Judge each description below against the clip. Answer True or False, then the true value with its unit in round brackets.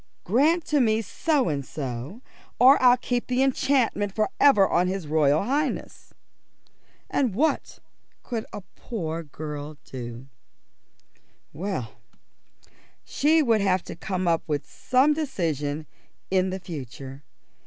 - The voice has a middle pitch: False (195 Hz)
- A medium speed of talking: False (120 wpm)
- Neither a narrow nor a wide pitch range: False (8.7 semitones)